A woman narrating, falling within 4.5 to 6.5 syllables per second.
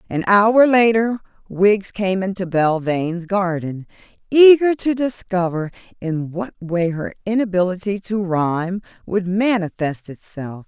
No: female; 4.1 syllables/s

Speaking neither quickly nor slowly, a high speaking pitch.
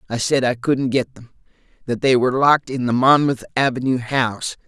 No: average, 180 wpm; low, 130 Hz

